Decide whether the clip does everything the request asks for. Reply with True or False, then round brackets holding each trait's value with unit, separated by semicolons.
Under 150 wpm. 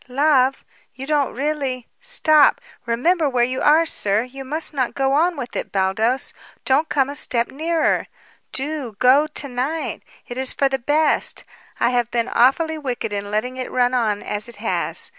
False (180 wpm)